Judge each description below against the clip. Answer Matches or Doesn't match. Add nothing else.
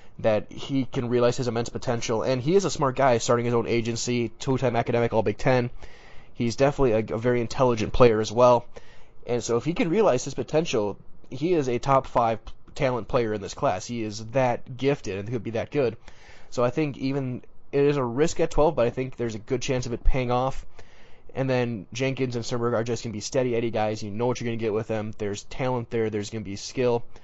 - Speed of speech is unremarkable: Doesn't match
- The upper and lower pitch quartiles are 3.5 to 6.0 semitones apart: Doesn't match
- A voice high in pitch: Doesn't match